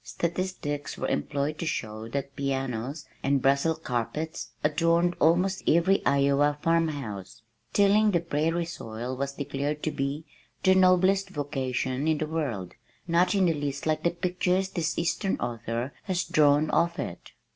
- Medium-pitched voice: Yes, medium, 150 Hz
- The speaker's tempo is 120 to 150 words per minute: Yes, average, 145 wpm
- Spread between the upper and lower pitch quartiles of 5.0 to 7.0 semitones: No, average, 3.7 semitones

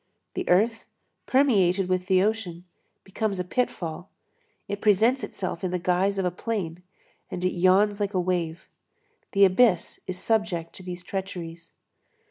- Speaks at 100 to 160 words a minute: Yes, average, 150 wpm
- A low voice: No, medium, 185 Hz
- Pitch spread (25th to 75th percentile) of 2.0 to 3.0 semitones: Yes, narrow, 2.5 semitones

